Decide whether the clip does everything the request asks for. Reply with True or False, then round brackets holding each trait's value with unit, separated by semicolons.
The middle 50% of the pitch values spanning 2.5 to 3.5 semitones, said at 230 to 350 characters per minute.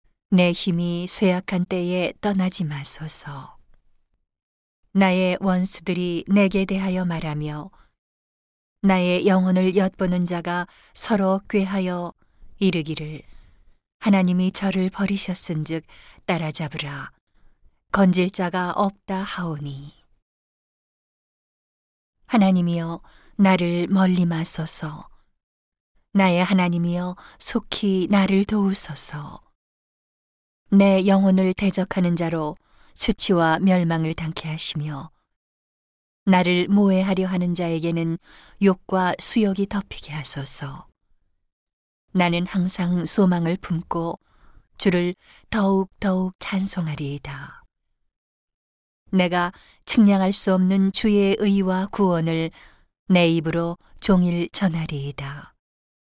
False (2.8 semitones; 205 characters per minute)